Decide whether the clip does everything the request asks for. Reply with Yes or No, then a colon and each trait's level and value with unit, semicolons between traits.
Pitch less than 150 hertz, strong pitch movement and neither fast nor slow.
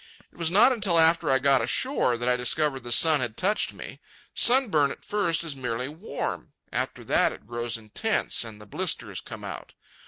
Yes: medium, 140 Hz; wide, 6.2 semitones; average, 190 wpm